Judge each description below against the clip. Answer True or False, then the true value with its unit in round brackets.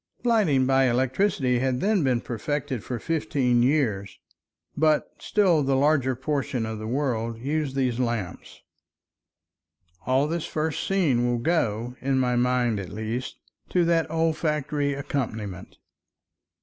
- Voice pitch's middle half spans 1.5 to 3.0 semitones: False (4.0 semitones)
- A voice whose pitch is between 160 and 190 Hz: False (130 Hz)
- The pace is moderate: False (130 wpm)